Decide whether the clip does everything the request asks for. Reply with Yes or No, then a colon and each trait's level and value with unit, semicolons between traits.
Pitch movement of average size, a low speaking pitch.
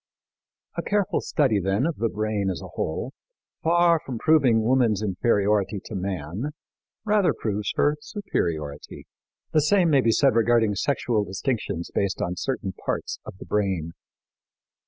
No: wide, 6.5 semitones; low, 110 Hz